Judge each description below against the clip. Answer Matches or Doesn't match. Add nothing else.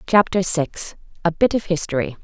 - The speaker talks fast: Doesn't match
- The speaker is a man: Doesn't match